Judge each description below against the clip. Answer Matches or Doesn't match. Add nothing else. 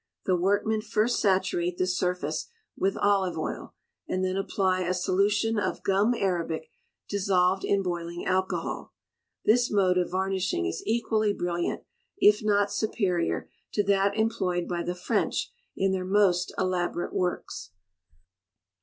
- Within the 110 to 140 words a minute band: Matches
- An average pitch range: Doesn't match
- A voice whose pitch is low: Doesn't match